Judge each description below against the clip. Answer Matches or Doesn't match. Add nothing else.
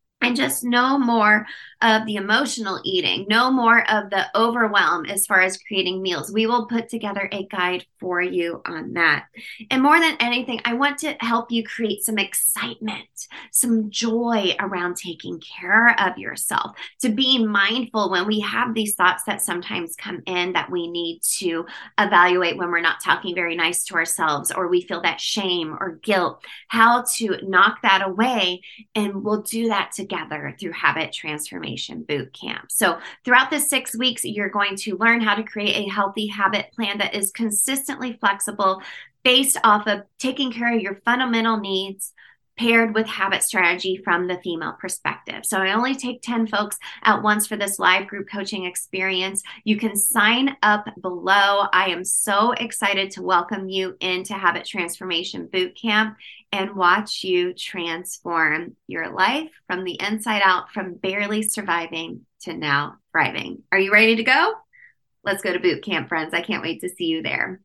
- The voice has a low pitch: Doesn't match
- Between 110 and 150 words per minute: Doesn't match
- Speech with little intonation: Doesn't match